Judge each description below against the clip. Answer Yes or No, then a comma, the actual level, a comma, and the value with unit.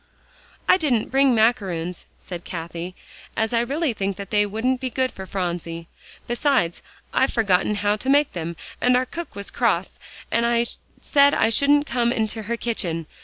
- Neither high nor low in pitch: No, high, 225 Hz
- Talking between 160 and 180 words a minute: Yes, average, 170 wpm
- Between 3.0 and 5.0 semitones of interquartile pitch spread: No, wide, 5.5 semitones